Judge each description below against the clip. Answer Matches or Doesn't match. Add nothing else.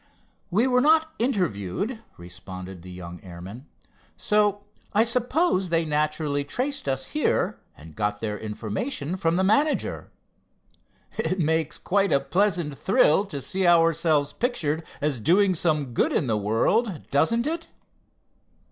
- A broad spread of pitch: Matches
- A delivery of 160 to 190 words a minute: Doesn't match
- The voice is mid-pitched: Matches